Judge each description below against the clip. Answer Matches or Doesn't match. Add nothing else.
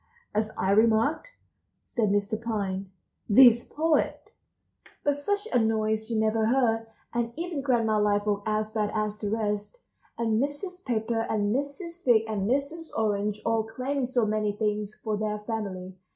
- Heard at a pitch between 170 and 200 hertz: Doesn't match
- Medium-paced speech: Matches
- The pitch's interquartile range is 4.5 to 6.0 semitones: Doesn't match